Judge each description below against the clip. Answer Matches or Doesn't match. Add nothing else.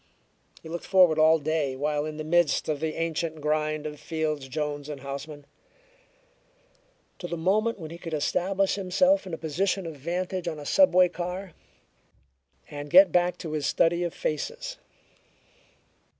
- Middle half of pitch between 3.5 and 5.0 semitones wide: Doesn't match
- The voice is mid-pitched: Matches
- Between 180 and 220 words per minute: Doesn't match